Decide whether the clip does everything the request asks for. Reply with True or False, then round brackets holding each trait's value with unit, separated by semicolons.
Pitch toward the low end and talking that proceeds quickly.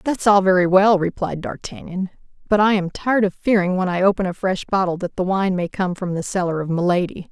False (190 Hz; 230 wpm)